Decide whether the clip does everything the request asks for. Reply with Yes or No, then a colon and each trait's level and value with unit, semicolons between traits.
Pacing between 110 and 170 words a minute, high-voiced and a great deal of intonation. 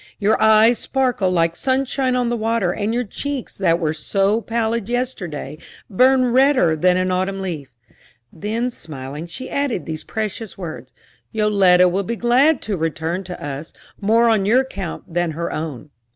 Yes: average, 165 wpm; high, 200 Hz; wide, 5.8 semitones